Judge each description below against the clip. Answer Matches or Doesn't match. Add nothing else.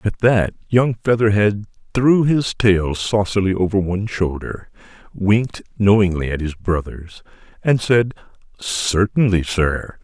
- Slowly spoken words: Matches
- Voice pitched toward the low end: Matches